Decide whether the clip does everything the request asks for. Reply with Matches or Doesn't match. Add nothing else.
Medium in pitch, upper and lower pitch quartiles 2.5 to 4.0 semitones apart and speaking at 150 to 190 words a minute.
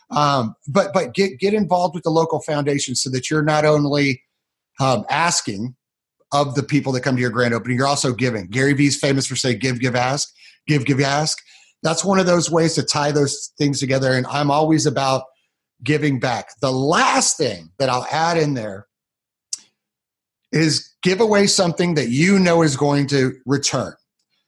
Matches